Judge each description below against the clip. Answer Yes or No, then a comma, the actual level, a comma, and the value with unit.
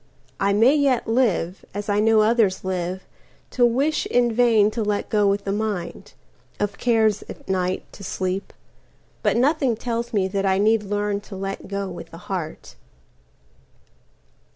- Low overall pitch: No, high, 205 Hz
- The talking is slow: No, average, 150 wpm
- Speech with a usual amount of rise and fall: Yes, average, 3.1 semitones